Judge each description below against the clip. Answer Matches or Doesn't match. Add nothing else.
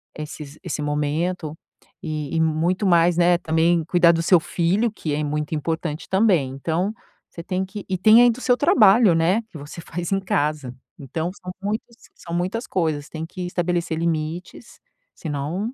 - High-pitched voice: Doesn't match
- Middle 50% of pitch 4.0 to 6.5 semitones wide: Doesn't match